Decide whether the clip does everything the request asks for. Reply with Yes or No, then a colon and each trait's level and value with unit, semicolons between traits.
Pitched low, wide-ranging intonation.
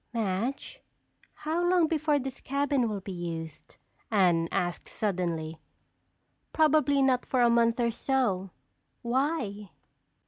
No: high, 235 Hz; wide, 7.0 semitones